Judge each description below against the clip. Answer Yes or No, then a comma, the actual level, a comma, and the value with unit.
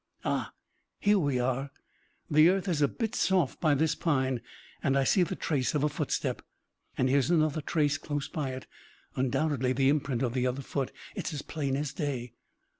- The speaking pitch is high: No, medium, 140 Hz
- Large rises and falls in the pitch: No, average, 3.0 semitones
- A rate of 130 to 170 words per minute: No, average, 190 wpm